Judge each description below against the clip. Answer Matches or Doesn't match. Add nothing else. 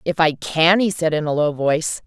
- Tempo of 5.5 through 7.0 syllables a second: Doesn't match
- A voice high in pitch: Doesn't match